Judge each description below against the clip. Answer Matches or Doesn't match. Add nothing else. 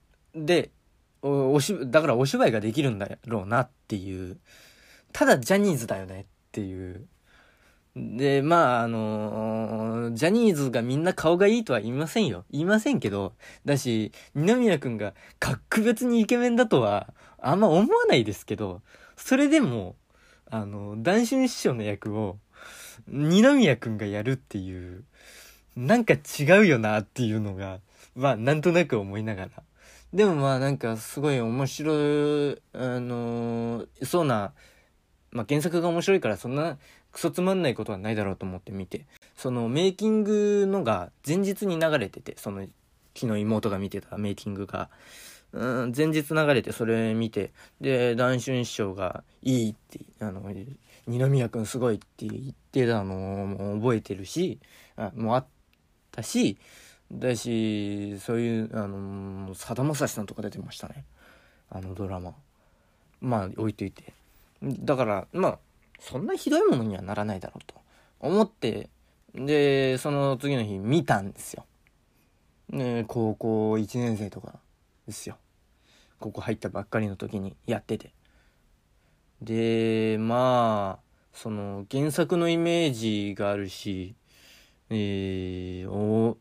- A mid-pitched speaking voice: Doesn't match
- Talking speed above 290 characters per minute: Doesn't match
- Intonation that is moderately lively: Doesn't match